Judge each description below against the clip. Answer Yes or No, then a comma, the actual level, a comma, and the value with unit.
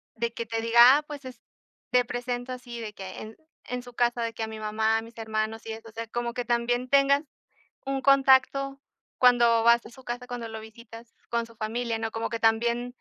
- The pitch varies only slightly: Yes, narrow, 1.8 semitones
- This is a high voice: Yes, high, 235 Hz